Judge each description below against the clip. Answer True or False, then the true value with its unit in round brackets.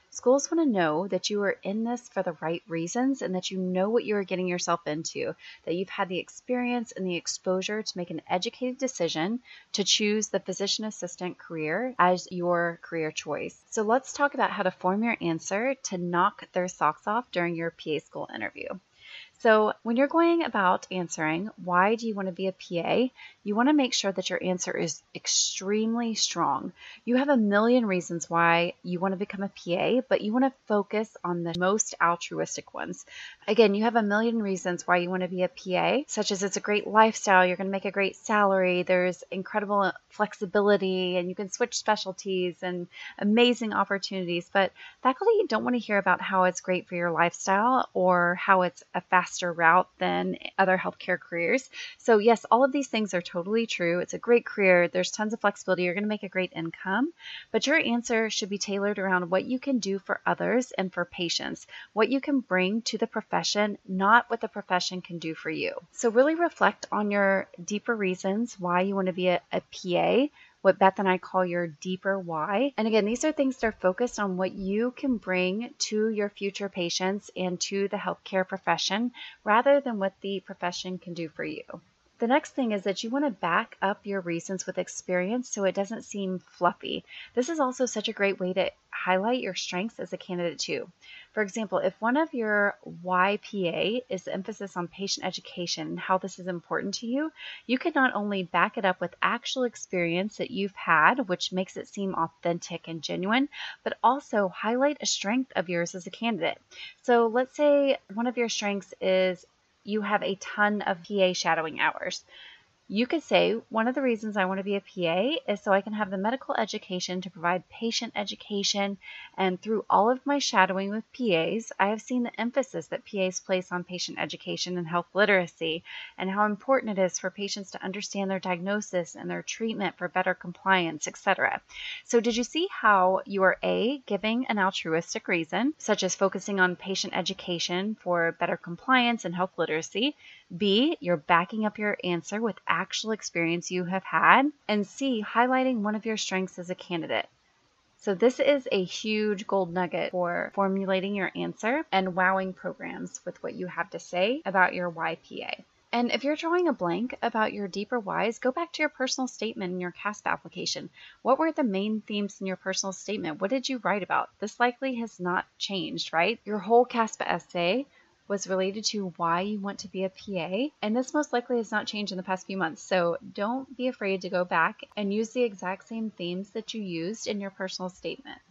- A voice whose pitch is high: True (195 Hz)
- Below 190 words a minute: False (200 wpm)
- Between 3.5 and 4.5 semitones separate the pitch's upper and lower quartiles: True (3.9 semitones)